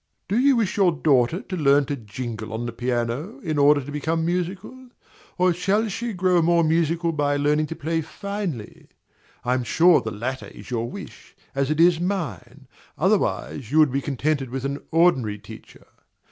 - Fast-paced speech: No, average, 180 wpm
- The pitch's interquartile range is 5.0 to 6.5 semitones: Yes, wide, 5.5 semitones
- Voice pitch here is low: No, medium, 155 Hz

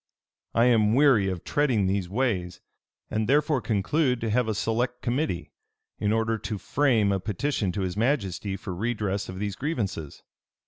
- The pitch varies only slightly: No, average, 4.4 semitones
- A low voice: Yes, low, 110 Hz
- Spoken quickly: No, average, 165 wpm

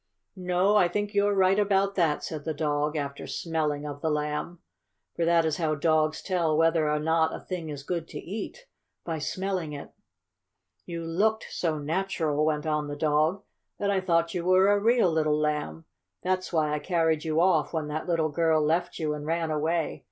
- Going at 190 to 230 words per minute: Yes, average, 195 wpm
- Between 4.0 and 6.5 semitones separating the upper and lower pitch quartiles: No, average, 3.2 semitones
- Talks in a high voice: No, medium, 165 Hz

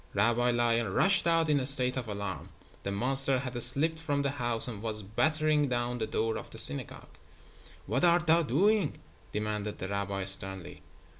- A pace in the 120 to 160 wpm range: No, average, 175 wpm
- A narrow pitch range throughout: No, wide, 5.4 semitones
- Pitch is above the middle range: No, low, 120 Hz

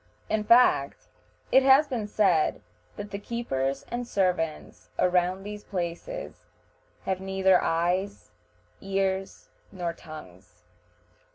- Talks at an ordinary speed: No, slow, 105 wpm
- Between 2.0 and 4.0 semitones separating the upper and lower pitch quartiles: Yes, average, 3.3 semitones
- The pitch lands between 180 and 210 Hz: Yes, high, 190 Hz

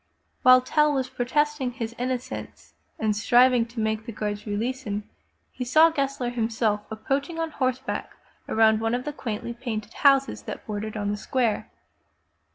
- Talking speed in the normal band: Yes, average, 165 wpm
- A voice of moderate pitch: No, high, 240 Hz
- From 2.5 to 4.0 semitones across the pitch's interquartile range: Yes, average, 3.3 semitones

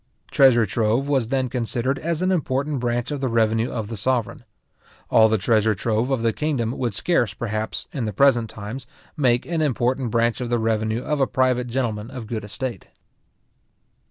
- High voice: No, low, 120 Hz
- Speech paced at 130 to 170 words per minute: No, average, 185 wpm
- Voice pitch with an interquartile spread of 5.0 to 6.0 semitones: No, average, 3.1 semitones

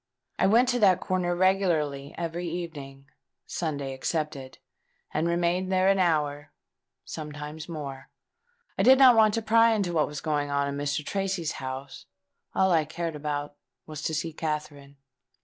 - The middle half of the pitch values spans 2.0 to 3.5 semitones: No, average, 4.2 semitones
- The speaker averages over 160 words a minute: No, average, 150 wpm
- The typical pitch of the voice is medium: Yes, medium, 160 Hz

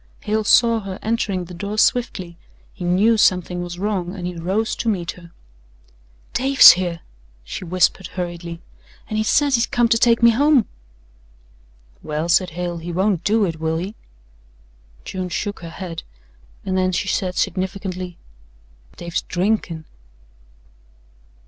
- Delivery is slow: No, average, 145 wpm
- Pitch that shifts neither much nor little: Yes, average, 3.7 semitones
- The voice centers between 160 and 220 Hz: Yes, medium, 185 Hz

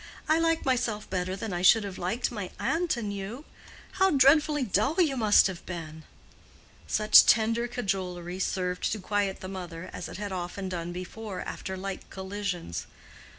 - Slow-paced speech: No, average, 165 wpm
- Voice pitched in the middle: No, high, 200 Hz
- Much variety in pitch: No, average, 4.4 semitones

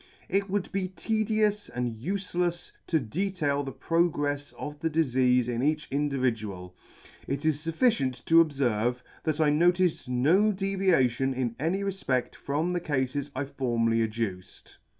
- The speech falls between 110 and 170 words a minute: Yes, average, 145 wpm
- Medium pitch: Yes, medium, 145 Hz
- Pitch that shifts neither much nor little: No, wide, 5.9 semitones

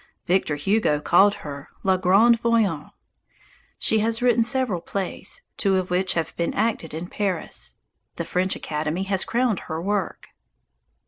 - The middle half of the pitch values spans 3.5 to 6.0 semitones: Yes, average, 4.5 semitones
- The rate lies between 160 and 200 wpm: No, average, 145 wpm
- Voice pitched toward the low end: No, high, 190 Hz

